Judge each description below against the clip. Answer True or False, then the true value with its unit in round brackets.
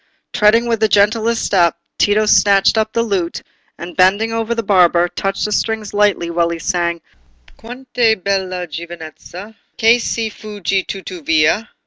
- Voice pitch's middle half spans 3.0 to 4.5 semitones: True (4.0 semitones)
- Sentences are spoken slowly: False (150 wpm)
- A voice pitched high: True (200 Hz)